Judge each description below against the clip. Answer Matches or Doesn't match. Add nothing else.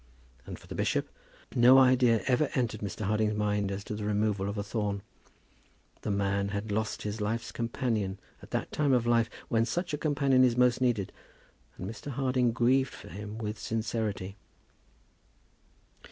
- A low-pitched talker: Matches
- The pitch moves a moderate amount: Matches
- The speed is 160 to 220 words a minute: Matches